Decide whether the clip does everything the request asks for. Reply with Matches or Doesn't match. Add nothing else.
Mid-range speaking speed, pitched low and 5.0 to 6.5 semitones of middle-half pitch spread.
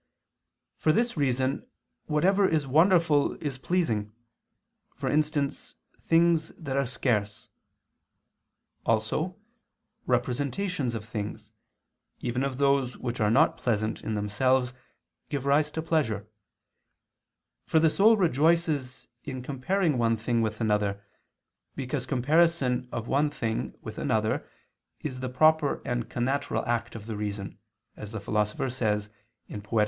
Doesn't match